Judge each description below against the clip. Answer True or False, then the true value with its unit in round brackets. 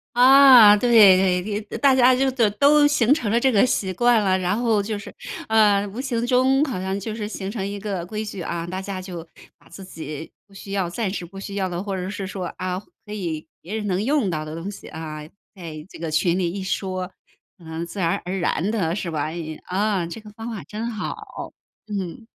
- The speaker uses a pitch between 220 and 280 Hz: False (200 Hz)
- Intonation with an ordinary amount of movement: True (3.7 semitones)